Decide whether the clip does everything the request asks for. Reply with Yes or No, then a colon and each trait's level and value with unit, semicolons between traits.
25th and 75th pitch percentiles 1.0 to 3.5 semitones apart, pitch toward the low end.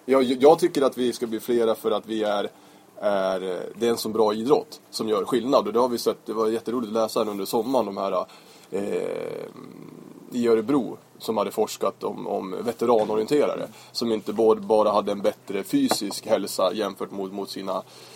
No: average, 4.0 semitones; low, 110 Hz